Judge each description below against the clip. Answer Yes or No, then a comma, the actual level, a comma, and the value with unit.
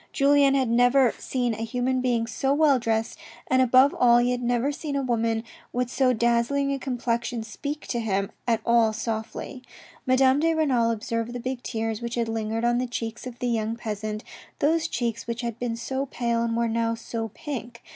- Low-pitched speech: No, high, 240 Hz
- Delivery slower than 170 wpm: No, average, 195 wpm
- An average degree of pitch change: No, narrow, 2.2 semitones